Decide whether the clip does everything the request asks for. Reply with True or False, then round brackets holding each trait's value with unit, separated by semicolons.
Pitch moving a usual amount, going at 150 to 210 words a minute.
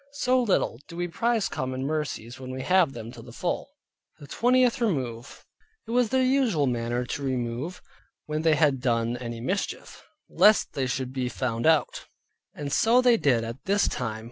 False (8.8 semitones; 180 wpm)